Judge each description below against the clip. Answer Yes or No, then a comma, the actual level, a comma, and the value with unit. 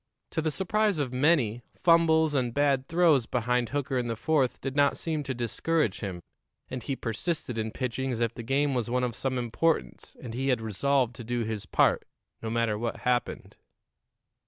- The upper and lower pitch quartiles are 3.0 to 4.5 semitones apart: Yes, average, 3.8 semitones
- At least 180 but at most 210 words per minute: Yes, average, 190 wpm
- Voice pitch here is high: No, low, 125 Hz